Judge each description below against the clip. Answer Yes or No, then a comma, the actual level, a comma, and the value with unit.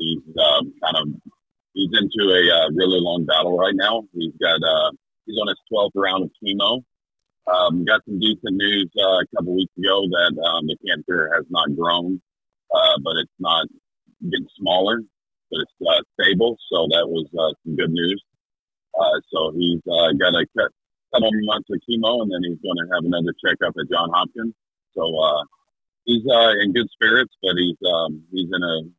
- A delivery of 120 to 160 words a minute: No, average, 190 wpm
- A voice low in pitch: Yes, very low, 95 Hz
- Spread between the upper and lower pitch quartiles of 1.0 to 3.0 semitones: No, average, 4.2 semitones